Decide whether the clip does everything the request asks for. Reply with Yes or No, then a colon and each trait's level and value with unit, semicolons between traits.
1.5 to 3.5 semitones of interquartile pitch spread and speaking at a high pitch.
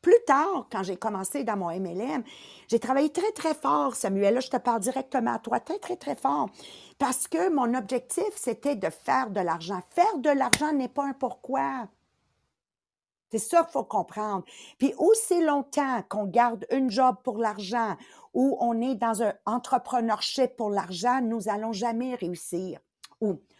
No: average, 4.8 semitones; very high, 250 Hz